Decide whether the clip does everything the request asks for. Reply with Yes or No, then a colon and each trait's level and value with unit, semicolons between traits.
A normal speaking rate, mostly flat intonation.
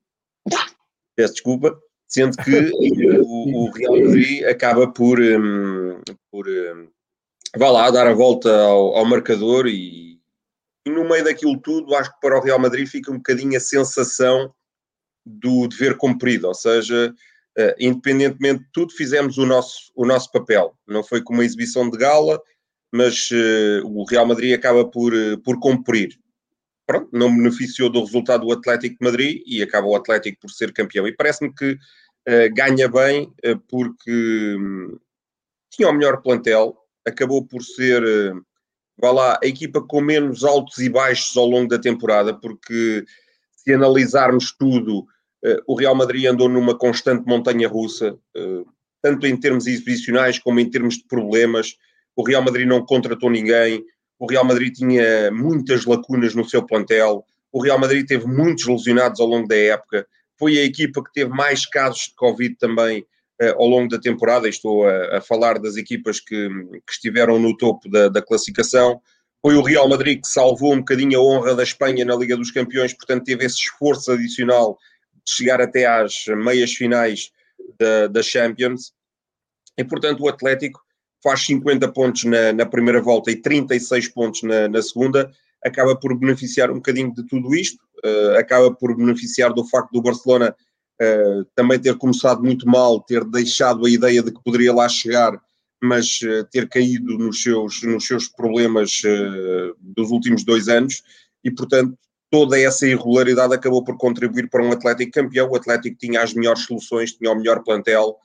Yes: average, 165 wpm; narrow, 2.2 semitones